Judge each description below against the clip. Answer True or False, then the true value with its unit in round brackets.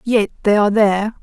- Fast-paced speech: False (195 wpm)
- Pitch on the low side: False (210 Hz)